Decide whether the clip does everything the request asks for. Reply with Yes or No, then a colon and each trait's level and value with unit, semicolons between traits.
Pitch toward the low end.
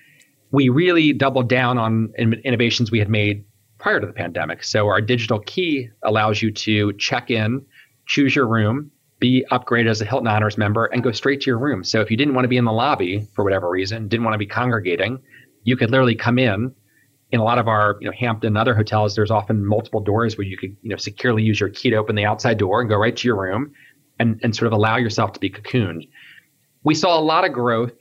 Yes: low, 115 Hz